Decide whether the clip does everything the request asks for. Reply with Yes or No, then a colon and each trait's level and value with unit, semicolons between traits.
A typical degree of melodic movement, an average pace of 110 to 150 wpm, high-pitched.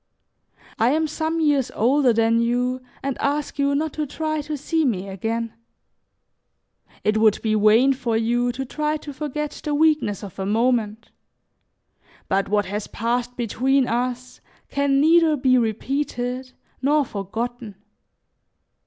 Yes: average, 4.4 semitones; average, 140 wpm; very high, 250 Hz